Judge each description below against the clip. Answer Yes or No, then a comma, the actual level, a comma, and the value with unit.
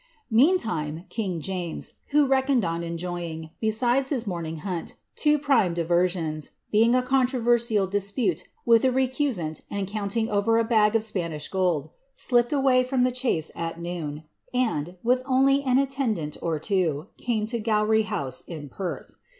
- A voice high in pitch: Yes, high, 210 Hz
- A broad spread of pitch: Yes, wide, 6.7 semitones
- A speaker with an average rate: Yes, average, 150 wpm